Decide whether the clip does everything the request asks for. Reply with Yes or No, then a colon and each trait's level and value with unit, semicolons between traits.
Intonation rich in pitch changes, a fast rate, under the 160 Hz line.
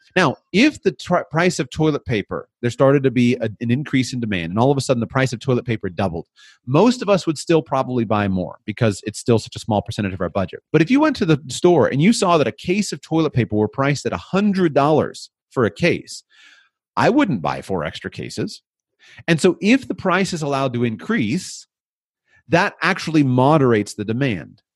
Yes: wide, 6.7 semitones; fast, 215 wpm; low, 135 Hz